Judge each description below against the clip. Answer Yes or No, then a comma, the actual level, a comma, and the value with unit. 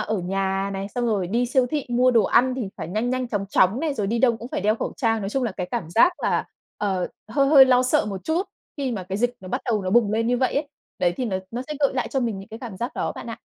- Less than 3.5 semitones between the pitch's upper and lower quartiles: No, average, 4.5 semitones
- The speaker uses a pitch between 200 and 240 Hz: Yes, high, 230 Hz